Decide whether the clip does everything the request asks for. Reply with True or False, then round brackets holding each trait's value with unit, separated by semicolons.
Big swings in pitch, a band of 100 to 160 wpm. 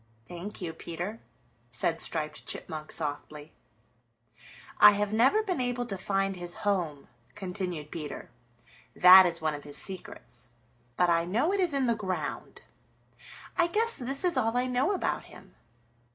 True (6.8 semitones; 150 wpm)